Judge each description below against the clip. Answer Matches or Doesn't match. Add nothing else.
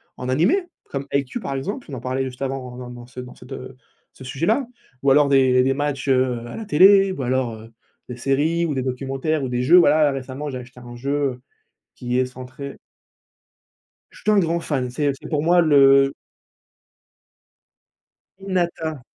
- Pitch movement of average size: Matches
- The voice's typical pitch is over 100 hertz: Matches